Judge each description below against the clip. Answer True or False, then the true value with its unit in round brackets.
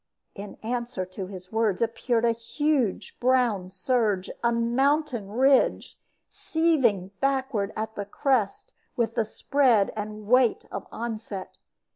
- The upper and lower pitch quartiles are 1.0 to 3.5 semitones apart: False (4.0 semitones)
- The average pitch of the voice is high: True (230 Hz)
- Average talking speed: False (125 wpm)